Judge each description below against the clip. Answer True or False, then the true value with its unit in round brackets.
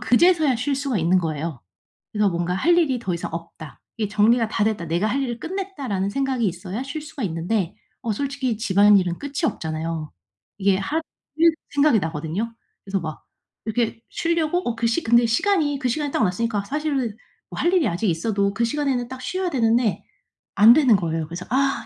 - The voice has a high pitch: True (230 Hz)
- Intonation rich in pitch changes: True (6.7 semitones)